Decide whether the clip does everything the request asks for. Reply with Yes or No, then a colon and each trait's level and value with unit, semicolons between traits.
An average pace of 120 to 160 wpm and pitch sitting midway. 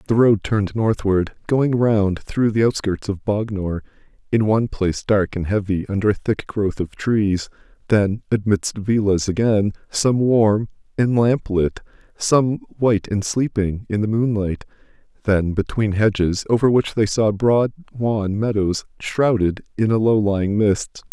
No: average, 155 wpm; low, 105 Hz